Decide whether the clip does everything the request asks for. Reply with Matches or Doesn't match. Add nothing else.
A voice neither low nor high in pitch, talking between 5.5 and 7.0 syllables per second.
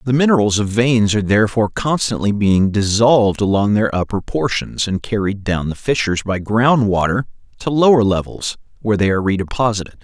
Doesn't match